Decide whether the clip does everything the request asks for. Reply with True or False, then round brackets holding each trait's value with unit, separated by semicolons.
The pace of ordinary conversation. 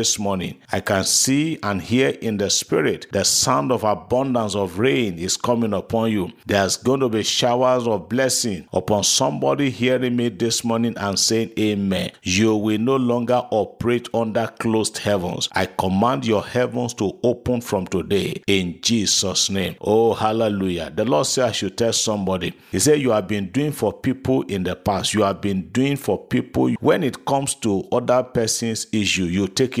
True (185 wpm)